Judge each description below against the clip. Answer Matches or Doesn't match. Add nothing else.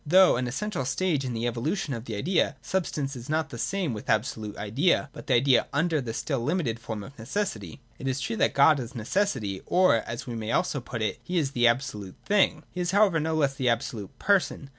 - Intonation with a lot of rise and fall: Matches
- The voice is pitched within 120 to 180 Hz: Matches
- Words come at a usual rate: Doesn't match